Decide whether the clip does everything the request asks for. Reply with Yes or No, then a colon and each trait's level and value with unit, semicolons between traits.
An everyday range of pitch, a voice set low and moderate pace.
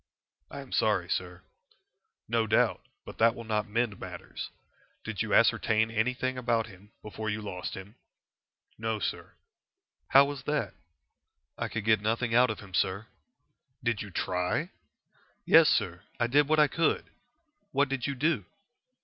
Yes: average, 3.4 semitones; low, 115 Hz; average, 155 wpm